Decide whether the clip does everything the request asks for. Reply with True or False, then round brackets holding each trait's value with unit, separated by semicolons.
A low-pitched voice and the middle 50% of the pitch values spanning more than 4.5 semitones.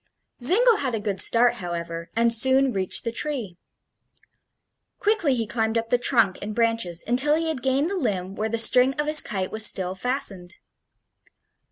False (230 Hz; 5.3 semitones)